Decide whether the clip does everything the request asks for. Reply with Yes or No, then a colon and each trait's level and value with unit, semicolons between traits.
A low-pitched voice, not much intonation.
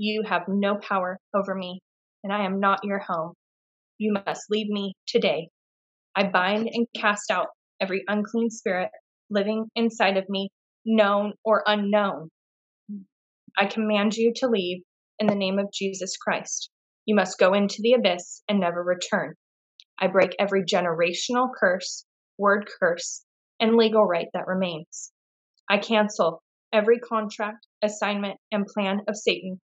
No: high, 200 Hz; narrow, 2.3 semitones